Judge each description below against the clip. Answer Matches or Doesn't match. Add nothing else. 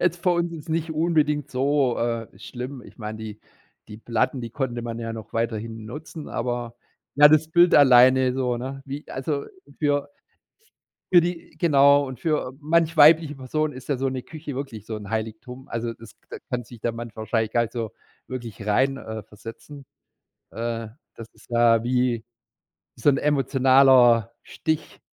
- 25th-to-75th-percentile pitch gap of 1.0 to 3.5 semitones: Doesn't match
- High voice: Doesn't match